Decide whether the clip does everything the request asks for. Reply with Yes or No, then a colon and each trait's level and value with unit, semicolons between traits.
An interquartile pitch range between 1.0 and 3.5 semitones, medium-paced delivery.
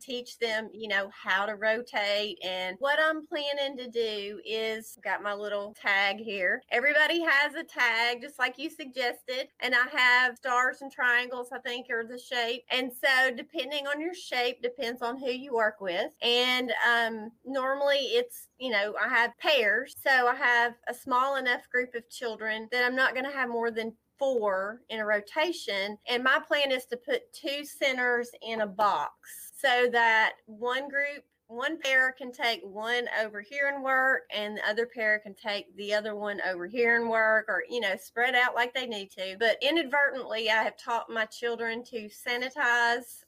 Yes: average, 3.2 semitones; average, 190 wpm